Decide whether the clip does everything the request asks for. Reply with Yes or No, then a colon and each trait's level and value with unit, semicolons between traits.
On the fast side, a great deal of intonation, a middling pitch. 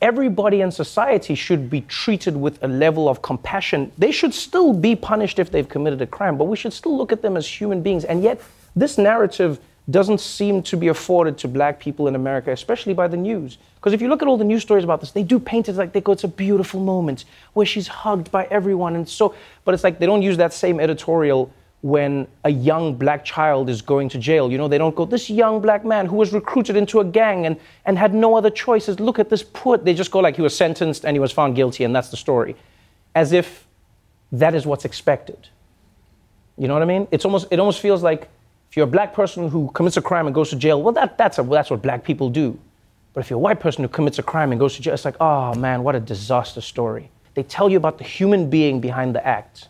Yes: fast, 250 wpm; wide, 6.2 semitones; medium, 170 Hz